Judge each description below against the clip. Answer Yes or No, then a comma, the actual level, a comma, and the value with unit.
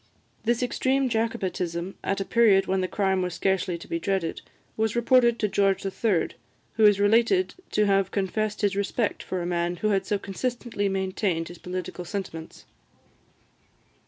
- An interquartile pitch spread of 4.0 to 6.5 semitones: No, average, 3.1 semitones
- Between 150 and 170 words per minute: Yes, average, 160 wpm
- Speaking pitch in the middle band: No, high, 195 Hz